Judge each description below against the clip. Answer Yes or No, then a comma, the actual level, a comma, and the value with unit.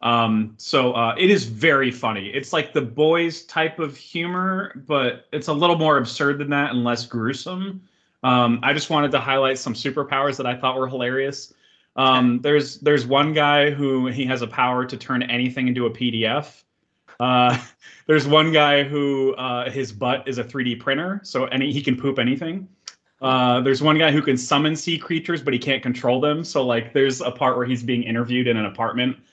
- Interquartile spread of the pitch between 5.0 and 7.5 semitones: No, average, 3.2 semitones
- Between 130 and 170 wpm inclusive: No, average, 200 wpm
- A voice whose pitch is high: No, low, 135 Hz